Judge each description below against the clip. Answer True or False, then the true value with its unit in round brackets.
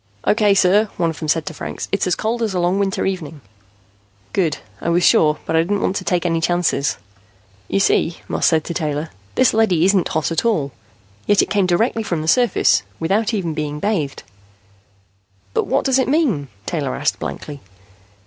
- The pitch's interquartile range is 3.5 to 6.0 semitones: True (4.5 semitones)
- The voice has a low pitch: False (175 Hz)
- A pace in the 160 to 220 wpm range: True (195 wpm)